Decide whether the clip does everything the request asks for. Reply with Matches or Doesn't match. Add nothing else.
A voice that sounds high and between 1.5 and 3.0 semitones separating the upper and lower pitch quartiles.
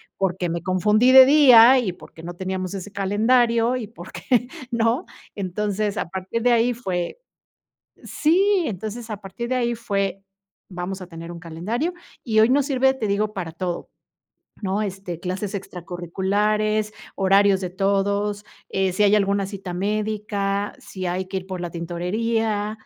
Doesn't match